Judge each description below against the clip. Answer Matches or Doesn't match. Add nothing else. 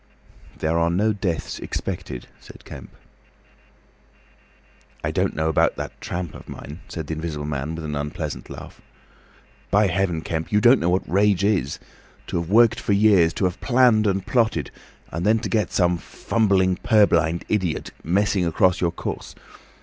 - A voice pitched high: Doesn't match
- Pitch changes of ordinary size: Matches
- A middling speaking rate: Matches